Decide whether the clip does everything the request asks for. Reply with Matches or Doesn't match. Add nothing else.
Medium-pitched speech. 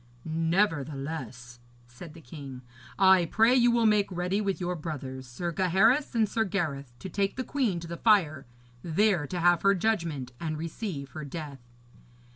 Matches